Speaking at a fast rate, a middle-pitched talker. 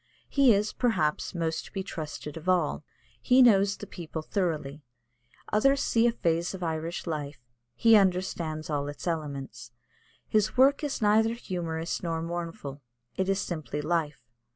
No: average, 155 wpm; medium, 170 Hz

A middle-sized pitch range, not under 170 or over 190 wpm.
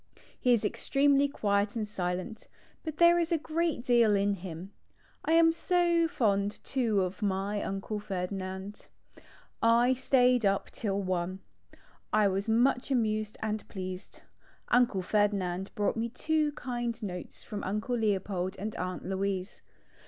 No: average, 4.3 semitones; average, 145 wpm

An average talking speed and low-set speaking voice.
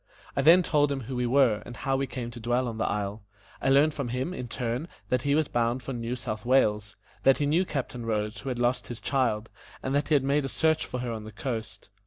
No: fast, 260 wpm; low, 125 Hz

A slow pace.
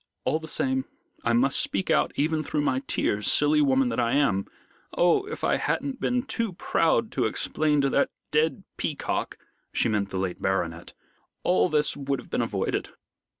No: average, 180 wpm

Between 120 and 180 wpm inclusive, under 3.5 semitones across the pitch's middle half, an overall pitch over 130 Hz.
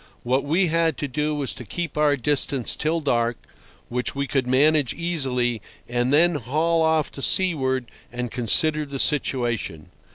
No: average, 160 wpm; average, 4.0 semitones; medium, 140 Hz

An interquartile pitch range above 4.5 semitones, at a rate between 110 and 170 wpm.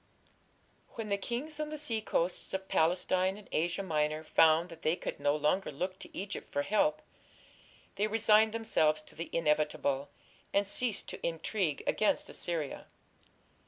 Yes: wide, 5.4 semitones; average, 150 wpm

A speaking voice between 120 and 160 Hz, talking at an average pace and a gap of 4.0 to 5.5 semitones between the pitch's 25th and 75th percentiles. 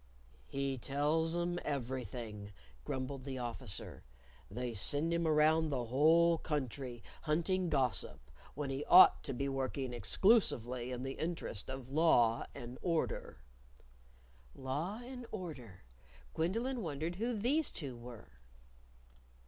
No: medium, 140 Hz; slow, 120 wpm; average, 5.2 semitones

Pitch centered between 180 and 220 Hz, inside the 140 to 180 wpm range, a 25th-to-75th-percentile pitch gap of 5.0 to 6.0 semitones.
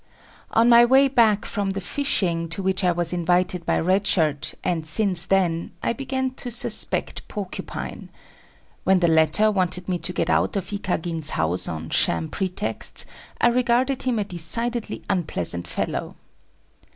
Yes: medium, 185 Hz; average, 155 wpm; average, 5.3 semitones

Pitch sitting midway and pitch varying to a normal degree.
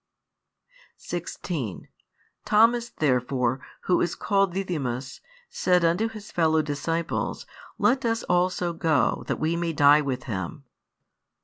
Yes: medium, 165 Hz; average, 4.7 semitones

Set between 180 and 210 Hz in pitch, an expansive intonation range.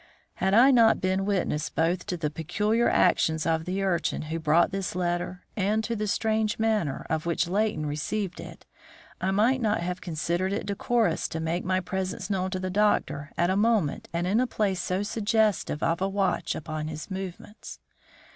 No: medium, 185 Hz; average, 3.7 semitones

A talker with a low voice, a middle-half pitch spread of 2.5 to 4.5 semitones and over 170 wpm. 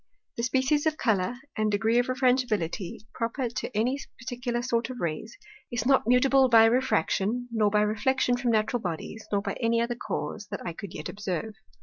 No: high, 230 Hz; average, 2.9 semitones; average, 185 wpm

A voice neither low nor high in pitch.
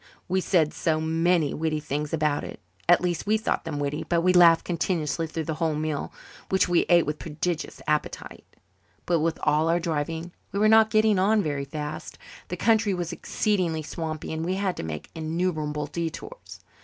Yes: medium, 165 Hz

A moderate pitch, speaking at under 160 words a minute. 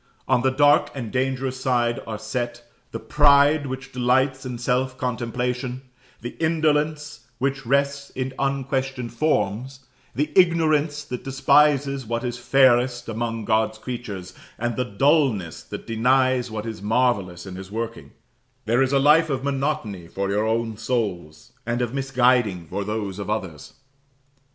No: low, 125 Hz; average, 145 wpm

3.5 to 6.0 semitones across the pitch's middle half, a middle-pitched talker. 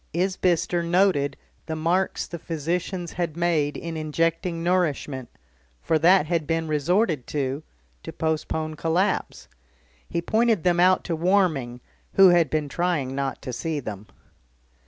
No: average, 2.9 semitones; medium, 165 Hz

